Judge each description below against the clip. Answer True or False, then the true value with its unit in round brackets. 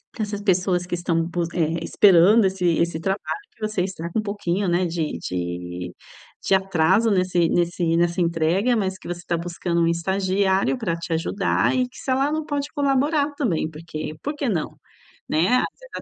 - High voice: False (180 Hz)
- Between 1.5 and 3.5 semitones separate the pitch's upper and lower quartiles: False (4.1 semitones)